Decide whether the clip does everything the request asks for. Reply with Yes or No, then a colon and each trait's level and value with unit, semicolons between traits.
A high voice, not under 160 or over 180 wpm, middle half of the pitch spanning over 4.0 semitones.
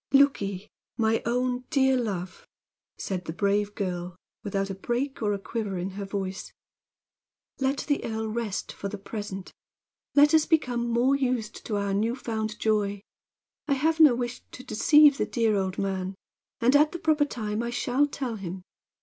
Yes: high, 220 Hz; average, 175 wpm; average, 4.7 semitones